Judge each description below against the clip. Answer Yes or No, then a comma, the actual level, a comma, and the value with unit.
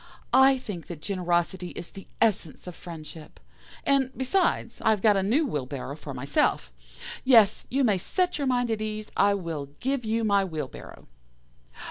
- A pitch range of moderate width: No, wide, 6.4 semitones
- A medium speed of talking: Yes, average, 165 wpm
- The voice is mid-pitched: No, high, 200 Hz